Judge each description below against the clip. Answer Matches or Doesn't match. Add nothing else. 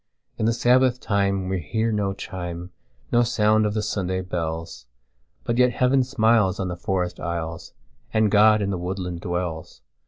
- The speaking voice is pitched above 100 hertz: Doesn't match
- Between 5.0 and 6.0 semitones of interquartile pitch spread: Doesn't match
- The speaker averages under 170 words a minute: Matches